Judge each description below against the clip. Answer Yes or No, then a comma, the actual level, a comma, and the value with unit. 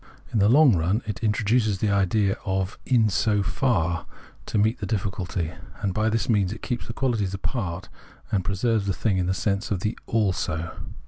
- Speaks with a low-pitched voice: Yes, low, 100 Hz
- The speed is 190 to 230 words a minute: Yes, fast, 205 wpm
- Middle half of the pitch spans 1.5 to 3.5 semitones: Yes, average, 2.9 semitones